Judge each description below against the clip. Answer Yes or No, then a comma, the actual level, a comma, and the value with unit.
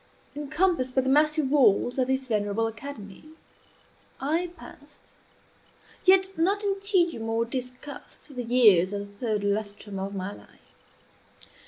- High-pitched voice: Yes, very high, 255 Hz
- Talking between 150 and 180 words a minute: No, slow, 135 wpm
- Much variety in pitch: Yes, wide, 6.6 semitones